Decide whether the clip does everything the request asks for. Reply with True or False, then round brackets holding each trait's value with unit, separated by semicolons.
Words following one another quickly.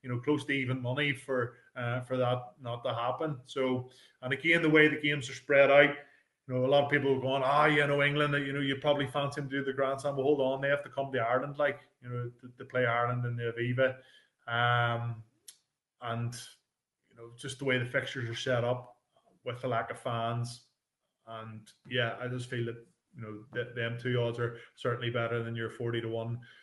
True (230 wpm)